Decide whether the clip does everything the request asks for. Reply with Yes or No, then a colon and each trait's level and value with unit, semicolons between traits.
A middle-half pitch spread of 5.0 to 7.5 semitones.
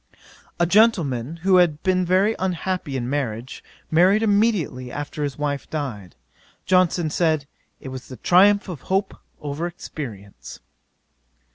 Yes: wide, 5.4 semitones